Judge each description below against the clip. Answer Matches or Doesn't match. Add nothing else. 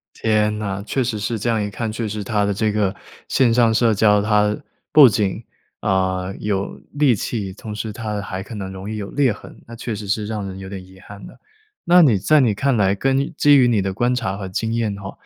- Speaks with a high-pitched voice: Doesn't match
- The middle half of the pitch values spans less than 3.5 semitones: Matches